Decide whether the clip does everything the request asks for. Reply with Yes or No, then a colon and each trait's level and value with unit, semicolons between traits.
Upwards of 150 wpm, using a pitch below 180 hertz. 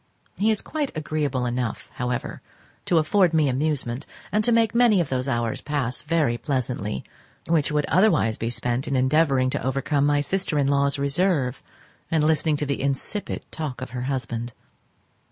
Yes: average, 170 wpm; medium, 140 Hz